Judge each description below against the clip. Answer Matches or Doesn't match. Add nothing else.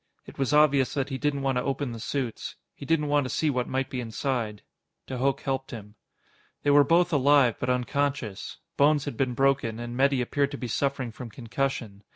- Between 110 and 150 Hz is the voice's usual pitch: Matches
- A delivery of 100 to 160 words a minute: Doesn't match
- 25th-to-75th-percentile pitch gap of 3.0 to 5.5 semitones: Doesn't match